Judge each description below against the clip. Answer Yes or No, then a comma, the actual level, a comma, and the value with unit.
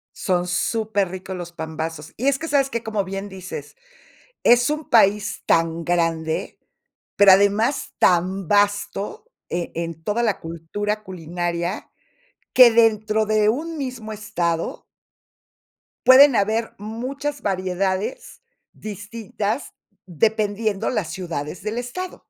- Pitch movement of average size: Yes, average, 4.4 semitones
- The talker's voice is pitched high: Yes, high, 205 Hz